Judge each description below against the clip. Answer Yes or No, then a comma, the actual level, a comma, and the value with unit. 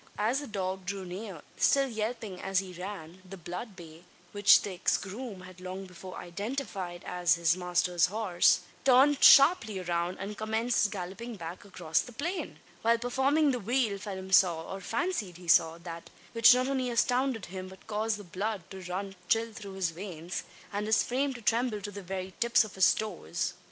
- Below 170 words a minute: No, average, 185 wpm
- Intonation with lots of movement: No, average, 4.1 semitones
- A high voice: Yes, high, 195 Hz